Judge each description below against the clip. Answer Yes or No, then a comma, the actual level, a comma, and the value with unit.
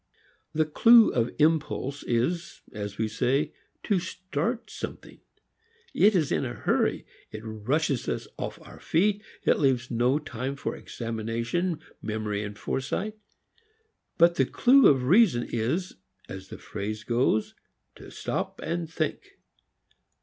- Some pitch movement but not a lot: No, wide, 7.0 semitones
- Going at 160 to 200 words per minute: No, slow, 135 wpm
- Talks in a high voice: No, low, 135 Hz